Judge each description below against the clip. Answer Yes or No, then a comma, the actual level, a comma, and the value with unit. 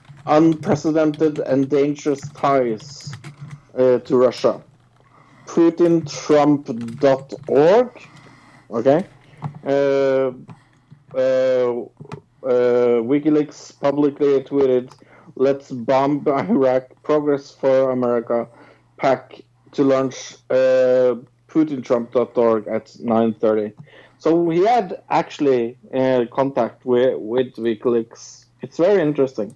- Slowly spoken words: Yes, slow, 80 wpm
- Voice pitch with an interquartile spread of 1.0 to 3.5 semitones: Yes, narrow, 2.6 semitones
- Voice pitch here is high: No, low, 135 Hz